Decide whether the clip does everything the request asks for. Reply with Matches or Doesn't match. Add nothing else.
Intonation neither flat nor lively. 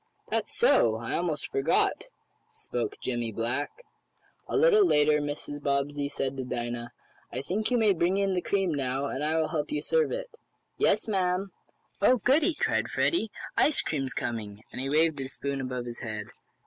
Doesn't match